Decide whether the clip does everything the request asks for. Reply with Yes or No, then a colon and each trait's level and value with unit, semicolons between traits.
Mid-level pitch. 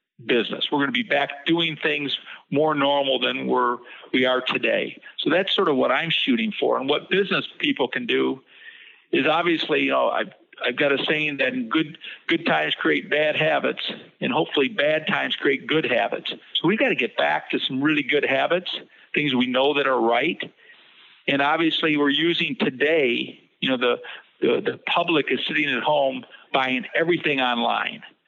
Yes: medium, 150 Hz